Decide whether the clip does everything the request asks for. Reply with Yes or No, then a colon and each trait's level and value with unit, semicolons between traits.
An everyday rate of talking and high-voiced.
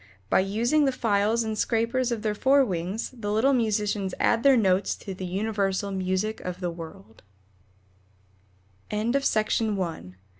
Yes: average, 150 wpm; high, 210 Hz